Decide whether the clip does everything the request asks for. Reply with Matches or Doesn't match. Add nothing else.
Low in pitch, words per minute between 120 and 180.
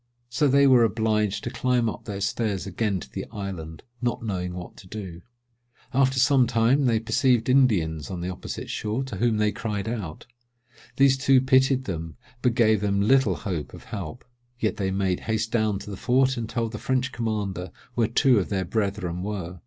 Doesn't match